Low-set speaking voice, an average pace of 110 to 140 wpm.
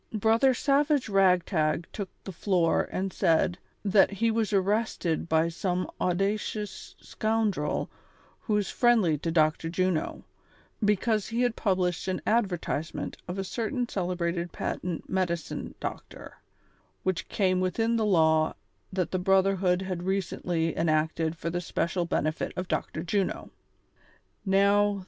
No: medium, 185 Hz; slow, 135 wpm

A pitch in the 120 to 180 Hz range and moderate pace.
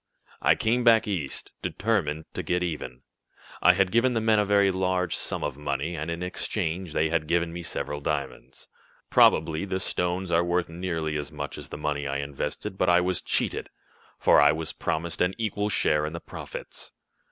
No: very low, 85 Hz; average, 190 wpm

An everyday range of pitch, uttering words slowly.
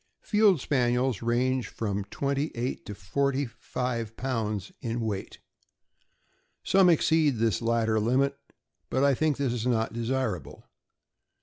Yes: average, 3.6 semitones; slow, 120 wpm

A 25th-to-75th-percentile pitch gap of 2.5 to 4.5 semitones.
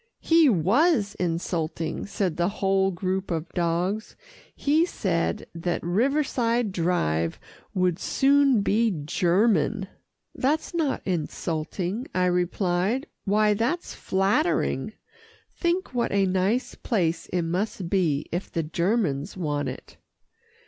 No: average, 5.2 semitones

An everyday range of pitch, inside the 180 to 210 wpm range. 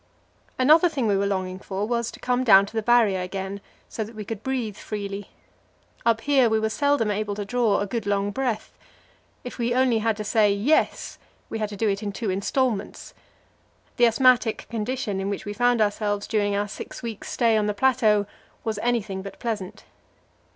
Yes: average, 3.0 semitones; average, 195 wpm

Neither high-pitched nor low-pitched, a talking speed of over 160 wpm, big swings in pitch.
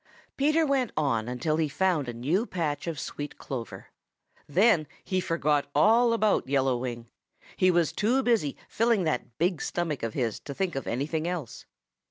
Yes: medium, 155 Hz; average, 170 wpm; wide, 6.1 semitones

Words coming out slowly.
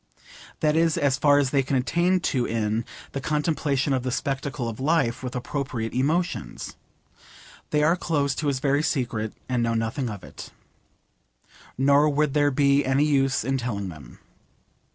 No: average, 165 wpm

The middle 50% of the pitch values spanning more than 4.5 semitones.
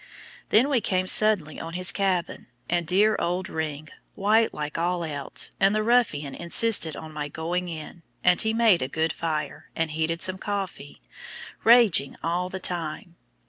No: average, 4.0 semitones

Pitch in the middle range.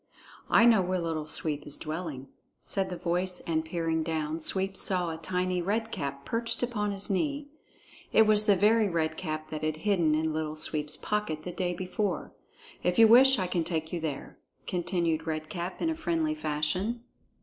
Yes: medium, 175 Hz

